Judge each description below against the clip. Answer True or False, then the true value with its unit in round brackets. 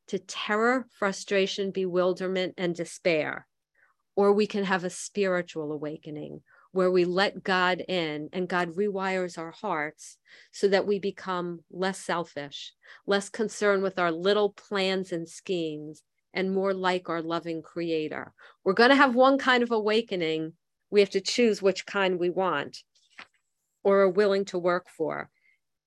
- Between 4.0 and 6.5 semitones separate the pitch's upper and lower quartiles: False (2.7 semitones)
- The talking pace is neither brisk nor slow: True (150 wpm)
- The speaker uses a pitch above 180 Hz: True (190 Hz)